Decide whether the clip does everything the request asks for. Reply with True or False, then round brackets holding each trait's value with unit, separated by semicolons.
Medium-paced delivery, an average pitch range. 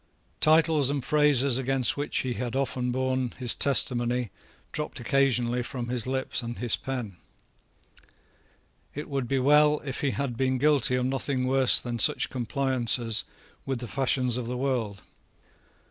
False (150 wpm; 2.0 semitones)